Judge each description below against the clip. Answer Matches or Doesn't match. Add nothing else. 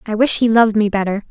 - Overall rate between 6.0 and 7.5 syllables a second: Matches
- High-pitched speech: Matches